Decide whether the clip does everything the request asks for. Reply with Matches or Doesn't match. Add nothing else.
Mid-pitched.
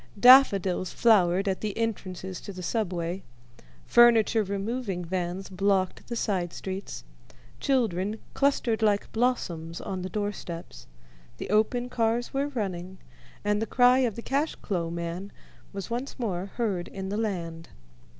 Doesn't match